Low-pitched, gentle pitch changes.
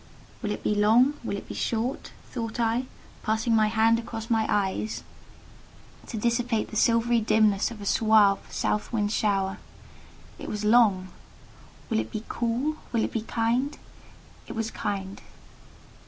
No: high, 220 Hz; narrow, 1.9 semitones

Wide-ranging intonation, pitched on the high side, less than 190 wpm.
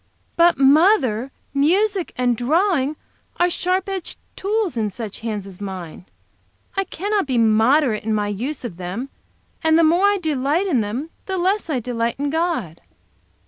Yes: wide, 8.0 semitones; very high, 280 Hz; average, 160 wpm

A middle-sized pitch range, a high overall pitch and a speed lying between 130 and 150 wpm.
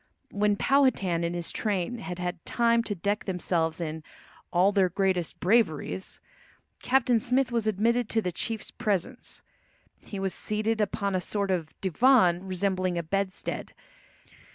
Yes: average, 4.0 semitones; high, 195 Hz; average, 145 wpm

